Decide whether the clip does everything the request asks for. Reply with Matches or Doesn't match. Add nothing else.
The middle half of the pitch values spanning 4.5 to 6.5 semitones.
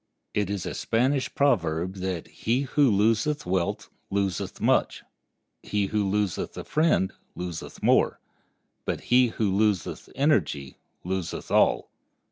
Matches